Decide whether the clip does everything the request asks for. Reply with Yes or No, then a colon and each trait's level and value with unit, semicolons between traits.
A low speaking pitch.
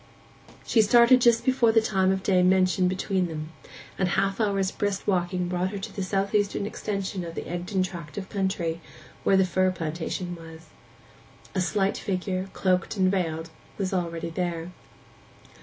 No: medium, 185 Hz